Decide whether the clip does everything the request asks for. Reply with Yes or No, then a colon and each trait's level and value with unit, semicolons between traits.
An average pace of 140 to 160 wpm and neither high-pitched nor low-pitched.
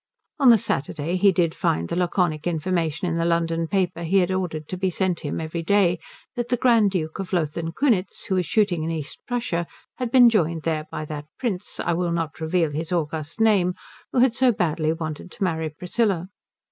No: fast, 205 wpm; medium, 175 Hz